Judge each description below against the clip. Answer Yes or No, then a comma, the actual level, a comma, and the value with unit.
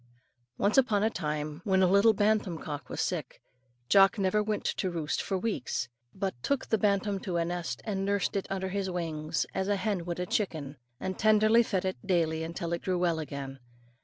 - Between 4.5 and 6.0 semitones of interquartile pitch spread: No, average, 3.5 semitones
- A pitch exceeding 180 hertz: Yes, high, 190 Hz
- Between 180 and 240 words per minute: Yes, average, 200 wpm